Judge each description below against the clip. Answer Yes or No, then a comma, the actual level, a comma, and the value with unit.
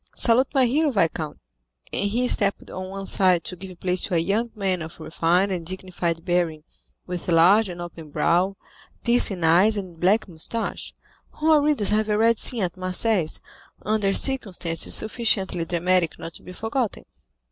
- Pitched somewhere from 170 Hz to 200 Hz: Yes, high, 190 Hz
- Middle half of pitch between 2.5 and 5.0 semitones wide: Yes, average, 4.0 semitones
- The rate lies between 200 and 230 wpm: No, average, 165 wpm